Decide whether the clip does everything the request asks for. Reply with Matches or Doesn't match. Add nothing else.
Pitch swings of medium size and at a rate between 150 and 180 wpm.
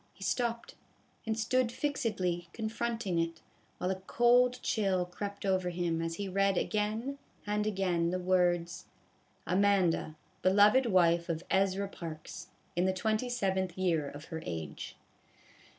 Doesn't match